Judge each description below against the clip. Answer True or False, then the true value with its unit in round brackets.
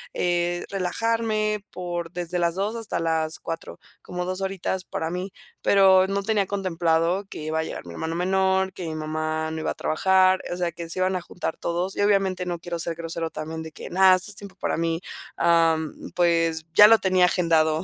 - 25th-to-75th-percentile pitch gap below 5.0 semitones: True (2.5 semitones)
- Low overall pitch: False (175 Hz)